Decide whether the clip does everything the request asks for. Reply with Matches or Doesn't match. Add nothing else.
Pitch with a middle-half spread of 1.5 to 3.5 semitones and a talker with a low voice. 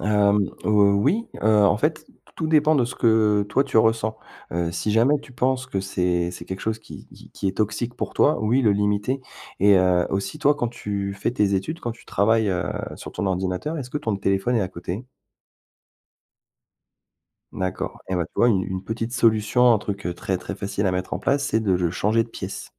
Doesn't match